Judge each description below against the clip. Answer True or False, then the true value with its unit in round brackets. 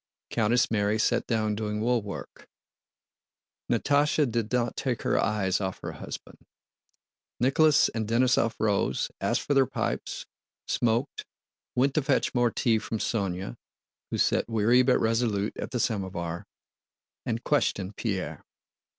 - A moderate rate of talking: False (125 wpm)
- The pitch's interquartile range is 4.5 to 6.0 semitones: False (2.9 semitones)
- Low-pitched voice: True (115 Hz)